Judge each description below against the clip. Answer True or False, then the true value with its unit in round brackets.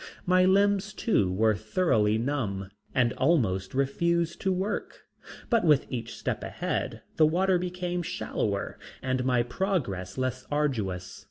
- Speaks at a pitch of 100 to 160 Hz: True (135 Hz)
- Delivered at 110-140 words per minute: True (135 wpm)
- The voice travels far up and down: True (8.6 semitones)